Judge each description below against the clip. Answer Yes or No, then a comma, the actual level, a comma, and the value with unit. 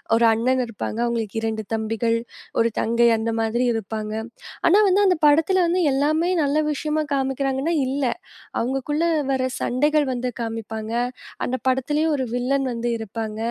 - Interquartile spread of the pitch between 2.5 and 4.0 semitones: No, average, 4.5 semitones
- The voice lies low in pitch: No, very high, 255 Hz